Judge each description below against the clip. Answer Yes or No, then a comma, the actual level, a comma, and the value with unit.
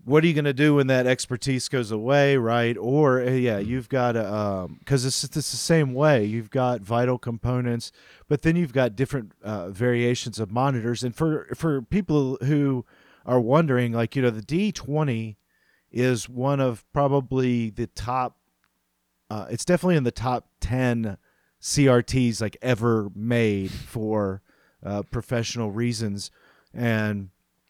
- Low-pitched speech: Yes, low, 125 Hz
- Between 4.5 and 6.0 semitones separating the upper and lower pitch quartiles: No, average, 3.4 semitones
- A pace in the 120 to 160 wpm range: Yes, average, 150 wpm